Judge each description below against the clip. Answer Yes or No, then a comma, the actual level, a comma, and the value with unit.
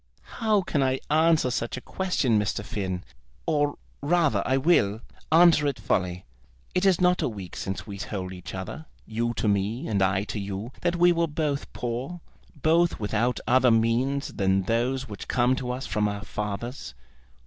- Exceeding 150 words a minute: Yes, average, 175 wpm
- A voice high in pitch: No, low, 120 Hz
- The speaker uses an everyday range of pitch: No, wide, 6.8 semitones